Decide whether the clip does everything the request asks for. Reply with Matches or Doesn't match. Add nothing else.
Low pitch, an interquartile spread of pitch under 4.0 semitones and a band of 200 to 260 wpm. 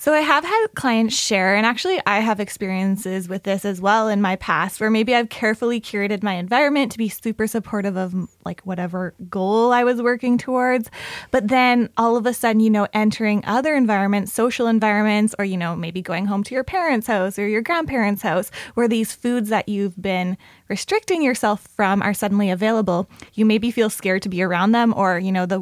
Doesn't match